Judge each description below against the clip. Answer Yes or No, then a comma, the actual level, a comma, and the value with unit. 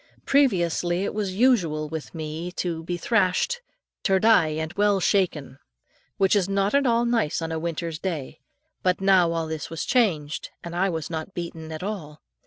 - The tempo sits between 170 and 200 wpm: Yes, average, 180 wpm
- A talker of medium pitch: Yes, medium, 175 Hz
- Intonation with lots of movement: No, average, 3.8 semitones